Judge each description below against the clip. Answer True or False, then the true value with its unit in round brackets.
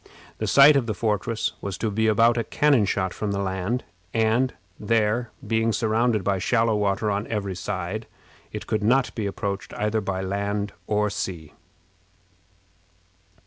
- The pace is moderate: True (150 wpm)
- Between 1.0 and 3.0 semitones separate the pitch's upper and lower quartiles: True (2.4 semitones)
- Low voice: True (105 Hz)